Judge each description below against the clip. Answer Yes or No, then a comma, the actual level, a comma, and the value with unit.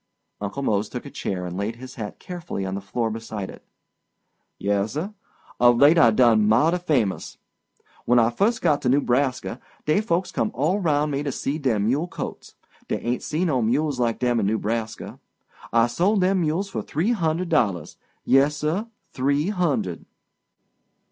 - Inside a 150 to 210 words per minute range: Yes, average, 165 wpm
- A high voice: No, low, 130 Hz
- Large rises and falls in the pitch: Yes, wide, 6.3 semitones